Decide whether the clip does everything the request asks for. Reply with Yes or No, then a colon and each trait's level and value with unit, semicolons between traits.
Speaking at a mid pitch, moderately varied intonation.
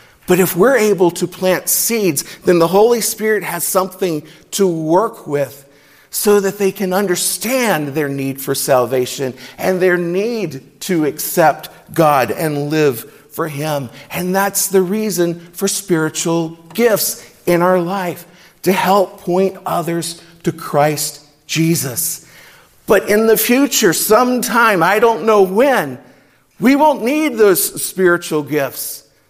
Yes: medium, 180 Hz; average, 4.7 semitones